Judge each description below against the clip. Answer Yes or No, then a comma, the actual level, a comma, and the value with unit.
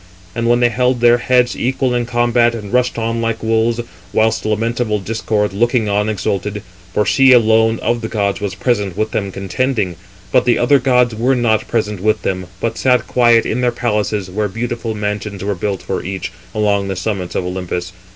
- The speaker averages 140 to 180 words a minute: No, average, 190 wpm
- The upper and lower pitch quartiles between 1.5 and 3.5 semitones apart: Yes, average, 2.8 semitones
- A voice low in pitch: Yes, low, 110 Hz